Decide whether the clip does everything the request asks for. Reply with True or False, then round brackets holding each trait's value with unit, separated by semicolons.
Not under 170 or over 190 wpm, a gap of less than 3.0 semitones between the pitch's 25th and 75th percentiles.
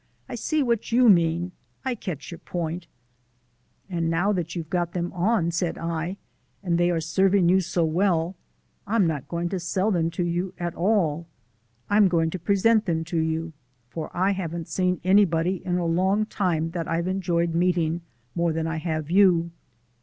True (180 wpm; 2.4 semitones)